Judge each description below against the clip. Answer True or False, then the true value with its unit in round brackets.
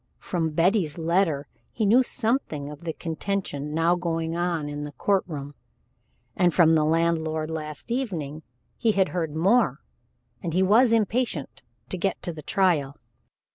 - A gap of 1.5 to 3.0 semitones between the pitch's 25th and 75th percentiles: False (4.0 semitones)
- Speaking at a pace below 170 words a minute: True (155 wpm)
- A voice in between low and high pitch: True (165 Hz)